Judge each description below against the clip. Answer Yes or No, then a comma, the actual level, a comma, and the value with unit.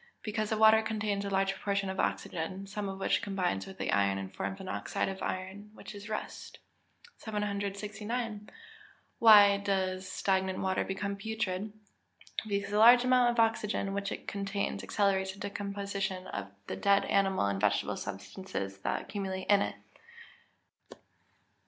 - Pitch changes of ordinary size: No, narrow, 1.7 semitones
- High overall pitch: Yes, high, 200 Hz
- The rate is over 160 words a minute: No, average, 150 wpm